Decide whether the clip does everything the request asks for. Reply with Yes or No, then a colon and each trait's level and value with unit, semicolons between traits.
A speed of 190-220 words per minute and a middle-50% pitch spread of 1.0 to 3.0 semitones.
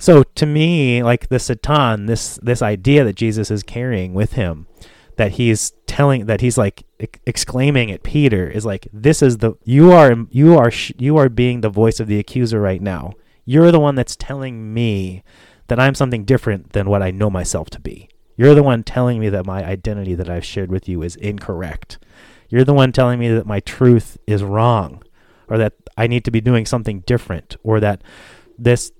No: average, 200 wpm; average, 3.8 semitones